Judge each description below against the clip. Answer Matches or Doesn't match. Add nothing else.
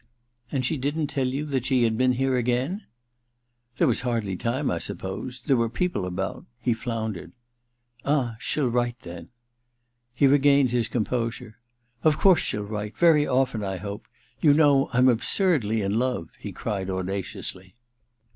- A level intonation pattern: Doesn't match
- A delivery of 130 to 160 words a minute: Doesn't match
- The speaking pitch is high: Doesn't match